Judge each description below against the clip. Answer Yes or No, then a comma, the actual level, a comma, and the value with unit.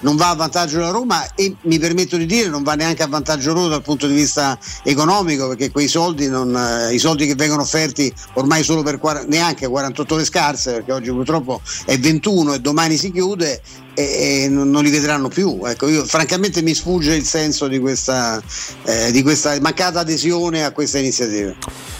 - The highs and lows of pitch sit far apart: No, average, 3.1 semitones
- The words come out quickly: Yes, fast, 195 wpm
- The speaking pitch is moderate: Yes, medium, 150 Hz